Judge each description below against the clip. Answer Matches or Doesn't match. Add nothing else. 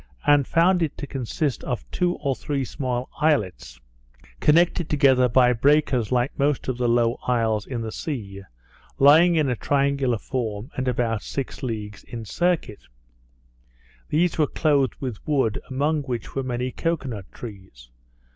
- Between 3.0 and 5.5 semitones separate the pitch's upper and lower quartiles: Matches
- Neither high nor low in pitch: Doesn't match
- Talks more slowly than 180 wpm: Matches